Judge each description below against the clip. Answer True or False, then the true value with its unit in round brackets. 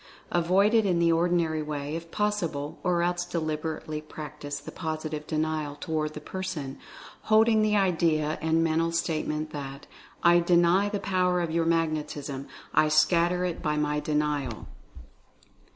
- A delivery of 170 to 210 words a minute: False (150 wpm)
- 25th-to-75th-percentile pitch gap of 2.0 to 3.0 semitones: True (2.5 semitones)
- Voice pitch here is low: False (160 Hz)